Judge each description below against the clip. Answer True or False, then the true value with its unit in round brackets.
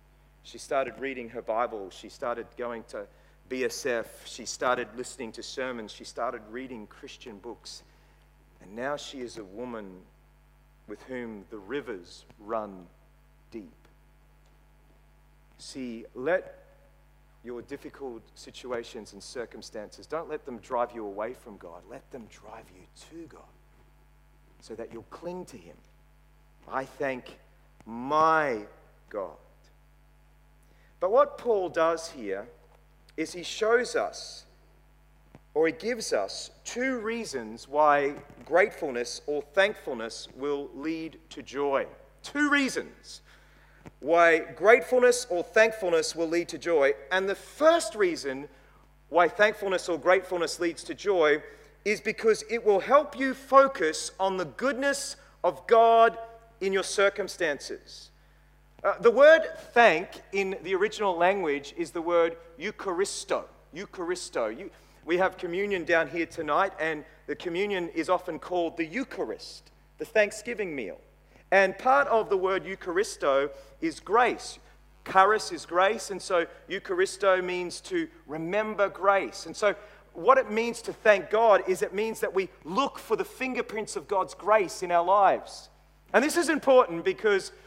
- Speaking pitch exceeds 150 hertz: True (185 Hz)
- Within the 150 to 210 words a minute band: False (135 wpm)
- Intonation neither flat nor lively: False (7.0 semitones)